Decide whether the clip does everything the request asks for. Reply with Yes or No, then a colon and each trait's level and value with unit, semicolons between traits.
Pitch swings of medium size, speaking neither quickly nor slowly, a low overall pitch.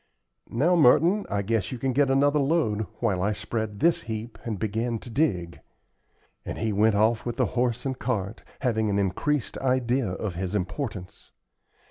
Yes: average, 4.4 semitones; average, 170 wpm; low, 115 Hz